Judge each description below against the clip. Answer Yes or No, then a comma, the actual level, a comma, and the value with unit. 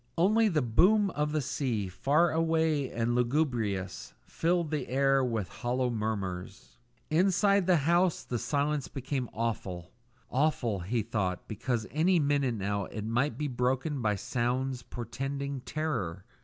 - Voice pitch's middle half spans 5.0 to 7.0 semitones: Yes, average, 5.3 semitones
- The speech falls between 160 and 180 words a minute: No, average, 140 wpm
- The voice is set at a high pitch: No, low, 130 Hz